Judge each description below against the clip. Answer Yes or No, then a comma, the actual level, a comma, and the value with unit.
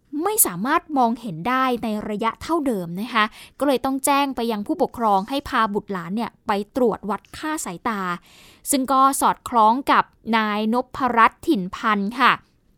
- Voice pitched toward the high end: Yes, high, 230 Hz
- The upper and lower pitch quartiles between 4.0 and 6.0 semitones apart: Yes, average, 4.3 semitones